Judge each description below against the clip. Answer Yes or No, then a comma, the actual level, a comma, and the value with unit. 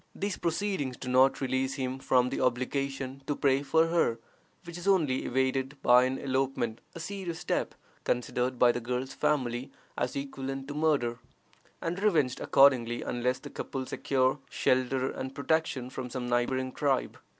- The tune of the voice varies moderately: No, narrow, 2.2 semitones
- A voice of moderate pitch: No, low, 130 Hz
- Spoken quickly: No, average, 160 wpm